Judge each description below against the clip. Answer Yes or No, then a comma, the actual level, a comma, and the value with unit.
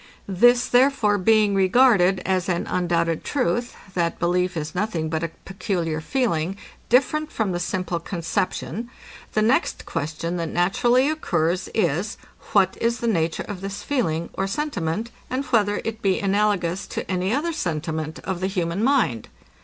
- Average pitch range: Yes, average, 5.0 semitones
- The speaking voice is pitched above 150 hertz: Yes, high, 190 Hz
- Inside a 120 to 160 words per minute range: Yes, average, 155 wpm